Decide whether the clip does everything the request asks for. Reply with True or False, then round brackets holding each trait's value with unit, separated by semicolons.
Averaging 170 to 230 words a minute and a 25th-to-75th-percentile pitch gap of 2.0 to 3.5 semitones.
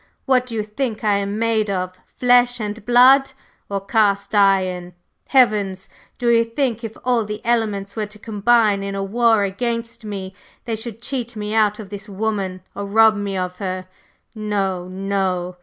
True (175 wpm; 2.8 semitones)